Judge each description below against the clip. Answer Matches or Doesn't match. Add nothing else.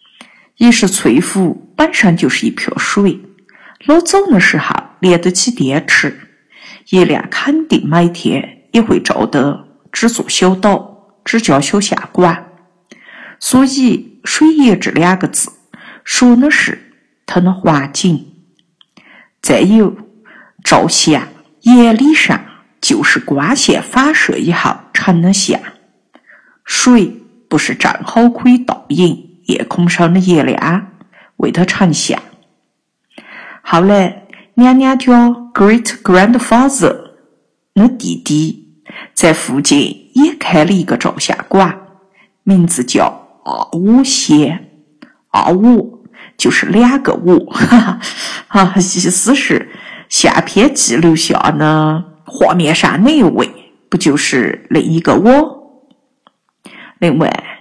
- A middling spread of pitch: Doesn't match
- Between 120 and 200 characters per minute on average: Matches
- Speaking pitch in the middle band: Doesn't match